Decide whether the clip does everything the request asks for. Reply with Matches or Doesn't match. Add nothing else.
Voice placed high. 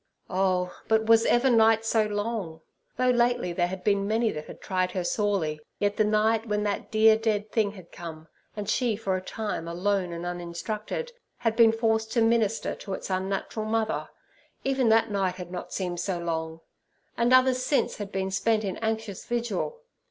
Matches